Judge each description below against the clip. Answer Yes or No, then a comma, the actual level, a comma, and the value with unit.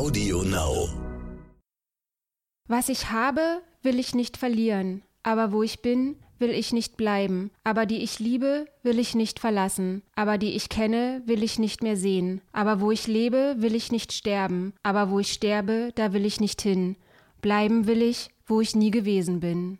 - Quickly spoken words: No, average, 175 wpm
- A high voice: Yes, high, 220 Hz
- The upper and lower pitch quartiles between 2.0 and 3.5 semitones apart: Yes, average, 2.9 semitones